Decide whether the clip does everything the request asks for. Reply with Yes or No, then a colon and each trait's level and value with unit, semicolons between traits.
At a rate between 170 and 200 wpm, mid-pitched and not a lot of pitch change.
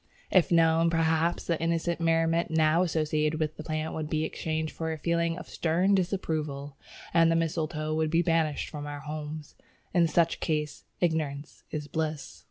Yes: average, 175 wpm; medium, 160 Hz; narrow, 1.3 semitones